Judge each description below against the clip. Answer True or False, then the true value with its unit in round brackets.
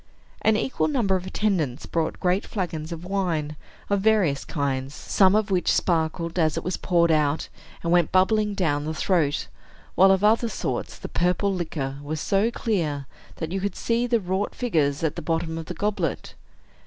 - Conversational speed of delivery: True (180 wpm)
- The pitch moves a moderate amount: True (4.1 semitones)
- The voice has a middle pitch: True (180 Hz)